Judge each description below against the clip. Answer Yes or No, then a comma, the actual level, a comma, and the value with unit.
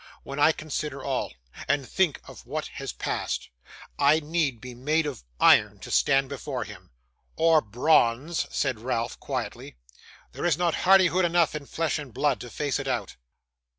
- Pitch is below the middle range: No, medium, 145 Hz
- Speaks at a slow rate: No, average, 165 wpm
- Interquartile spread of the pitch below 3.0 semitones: No, average, 3.8 semitones